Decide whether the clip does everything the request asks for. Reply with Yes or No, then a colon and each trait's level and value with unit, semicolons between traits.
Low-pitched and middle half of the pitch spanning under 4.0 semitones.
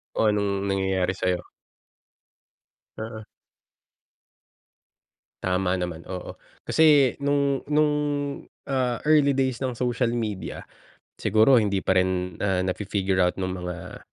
No: low, 100 Hz; wide, 5.5 semitones